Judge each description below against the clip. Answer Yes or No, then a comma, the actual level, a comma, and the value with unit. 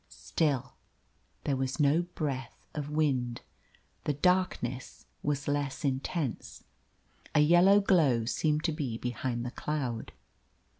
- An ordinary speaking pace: No, slow, 115 wpm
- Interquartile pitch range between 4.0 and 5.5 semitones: No, average, 3.3 semitones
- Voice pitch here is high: No, medium, 145 Hz